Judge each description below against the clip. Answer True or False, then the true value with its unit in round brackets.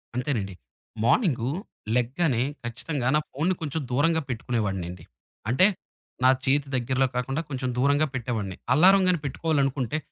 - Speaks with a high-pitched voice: False (130 Hz)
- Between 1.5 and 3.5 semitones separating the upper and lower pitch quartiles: False (4.0 semitones)